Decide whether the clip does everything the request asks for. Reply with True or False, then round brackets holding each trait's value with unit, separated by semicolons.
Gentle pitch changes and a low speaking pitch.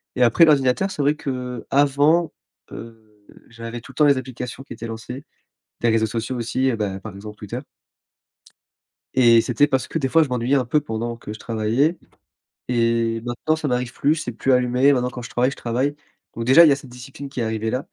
False (3.1 semitones; 125 Hz)